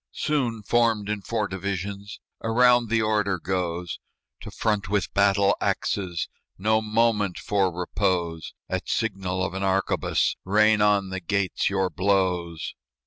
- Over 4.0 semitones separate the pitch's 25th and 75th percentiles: No, narrow, 2.5 semitones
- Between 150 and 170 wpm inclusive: No, slow, 135 wpm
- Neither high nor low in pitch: No, low, 100 Hz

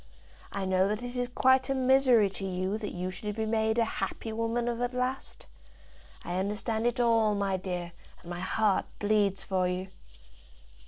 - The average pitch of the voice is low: No, high, 215 Hz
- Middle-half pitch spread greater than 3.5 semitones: Yes, average, 4.1 semitones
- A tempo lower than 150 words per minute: No, average, 180 wpm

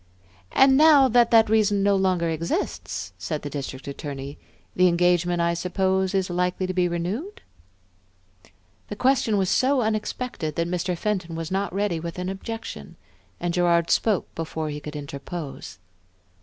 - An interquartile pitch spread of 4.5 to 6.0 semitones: No, average, 3.9 semitones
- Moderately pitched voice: Yes, medium, 180 Hz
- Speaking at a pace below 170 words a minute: Yes, average, 155 wpm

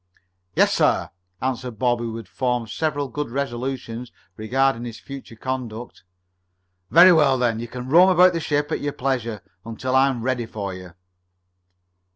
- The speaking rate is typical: Yes, average, 160 wpm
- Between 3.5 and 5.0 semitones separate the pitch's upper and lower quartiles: No, average, 3.1 semitones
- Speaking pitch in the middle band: No, low, 125 Hz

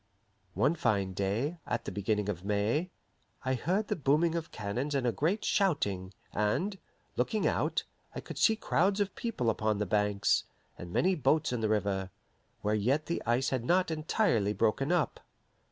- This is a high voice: No, low, 125 Hz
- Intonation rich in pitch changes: Yes, wide, 8.4 semitones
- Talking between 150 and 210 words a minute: Yes, average, 170 wpm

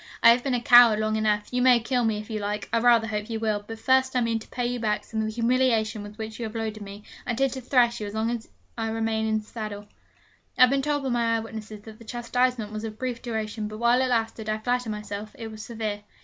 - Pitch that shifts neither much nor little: No, narrow, 2.0 semitones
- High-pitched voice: Yes, high, 225 Hz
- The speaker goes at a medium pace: No, fast, 275 wpm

